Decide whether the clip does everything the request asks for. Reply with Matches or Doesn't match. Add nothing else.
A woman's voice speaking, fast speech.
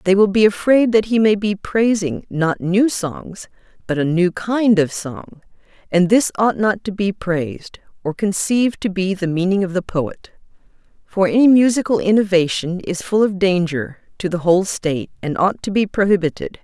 Doesn't match